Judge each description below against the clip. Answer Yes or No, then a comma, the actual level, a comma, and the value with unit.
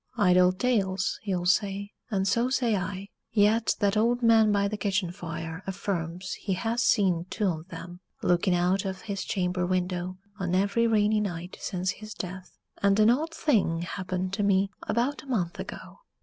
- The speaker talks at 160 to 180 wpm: Yes, average, 175 wpm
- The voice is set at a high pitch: Yes, high, 195 Hz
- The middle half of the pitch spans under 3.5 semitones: Yes, average, 2.8 semitones